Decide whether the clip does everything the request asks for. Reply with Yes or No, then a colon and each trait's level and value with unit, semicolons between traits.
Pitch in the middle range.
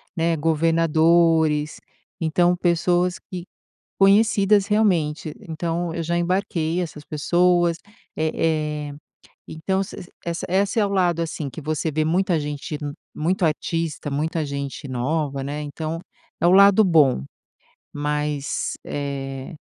Yes: medium, 165 Hz